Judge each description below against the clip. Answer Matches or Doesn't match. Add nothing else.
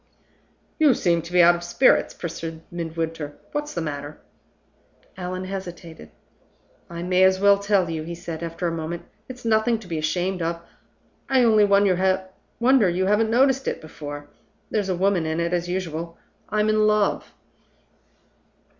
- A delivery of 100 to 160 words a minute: Matches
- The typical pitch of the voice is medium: Matches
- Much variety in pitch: Doesn't match